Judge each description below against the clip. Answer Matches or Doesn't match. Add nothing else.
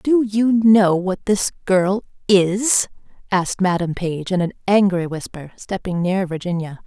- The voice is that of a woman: Matches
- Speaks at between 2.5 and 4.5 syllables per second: Matches